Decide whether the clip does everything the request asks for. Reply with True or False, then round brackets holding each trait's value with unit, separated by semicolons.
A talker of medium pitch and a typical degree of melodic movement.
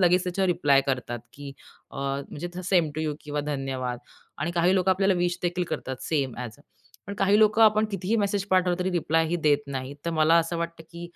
True (170 Hz; 4.5 semitones)